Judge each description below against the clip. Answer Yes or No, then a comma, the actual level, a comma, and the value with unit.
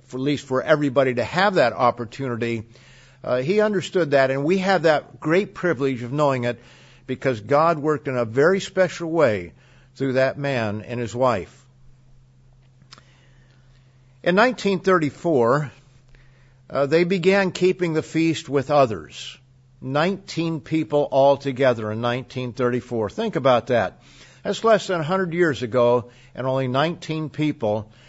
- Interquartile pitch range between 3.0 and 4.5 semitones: Yes, average, 3.9 semitones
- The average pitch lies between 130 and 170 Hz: Yes, low, 135 Hz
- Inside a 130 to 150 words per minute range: Yes, average, 140 wpm